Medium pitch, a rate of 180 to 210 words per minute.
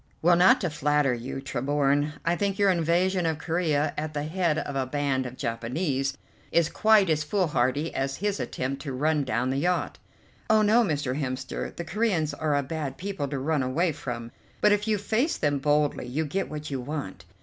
Yes: medium, 150 Hz; average, 195 wpm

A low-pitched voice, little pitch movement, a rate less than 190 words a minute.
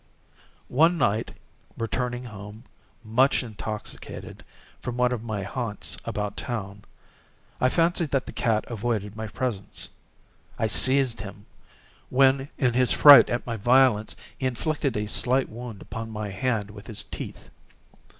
No: low, 115 Hz; average, 3.5 semitones; average, 140 wpm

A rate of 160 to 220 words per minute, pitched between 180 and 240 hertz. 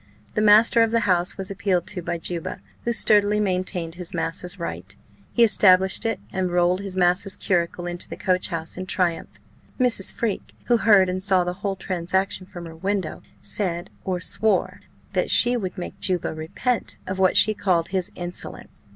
Yes: average, 180 wpm; medium, 185 Hz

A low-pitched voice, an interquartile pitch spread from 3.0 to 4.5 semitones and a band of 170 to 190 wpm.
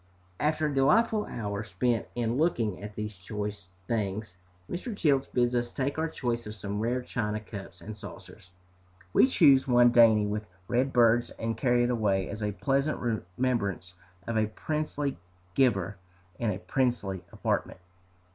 No: low, 115 Hz; average, 4.0 semitones; average, 155 wpm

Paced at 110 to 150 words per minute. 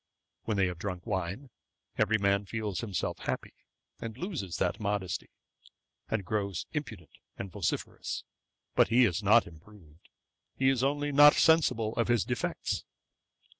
Yes: average, 140 wpm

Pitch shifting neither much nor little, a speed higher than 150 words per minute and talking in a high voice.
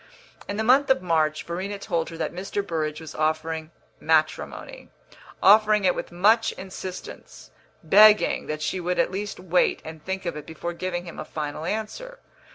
No: average, 4.1 semitones; average, 170 wpm; medium, 180 Hz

